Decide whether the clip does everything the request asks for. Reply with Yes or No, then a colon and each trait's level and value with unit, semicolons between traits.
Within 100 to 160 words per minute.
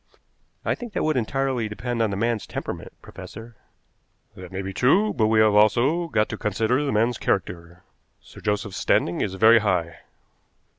No: average, 170 wpm